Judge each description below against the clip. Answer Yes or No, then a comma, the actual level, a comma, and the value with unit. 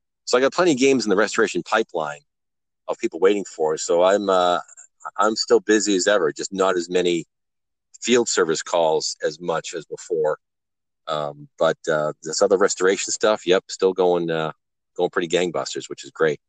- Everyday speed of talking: Yes, average, 185 wpm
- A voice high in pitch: No, low, 105 Hz